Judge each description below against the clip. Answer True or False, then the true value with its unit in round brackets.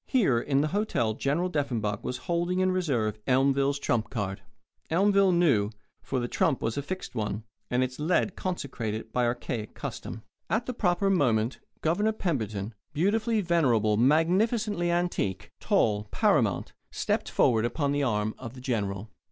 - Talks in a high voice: False (140 Hz)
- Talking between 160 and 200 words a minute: False (150 wpm)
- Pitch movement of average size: False (7.9 semitones)